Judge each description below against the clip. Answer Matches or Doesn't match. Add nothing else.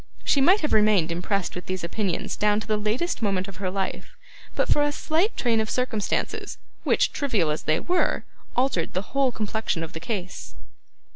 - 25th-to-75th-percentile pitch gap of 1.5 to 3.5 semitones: Doesn't match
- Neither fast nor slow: Matches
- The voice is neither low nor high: Doesn't match